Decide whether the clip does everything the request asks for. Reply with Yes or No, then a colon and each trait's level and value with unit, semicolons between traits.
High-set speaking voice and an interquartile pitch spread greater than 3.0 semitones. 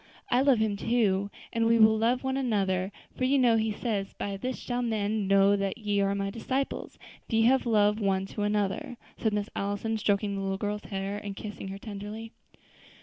No: high, 210 Hz; narrow, 2.5 semitones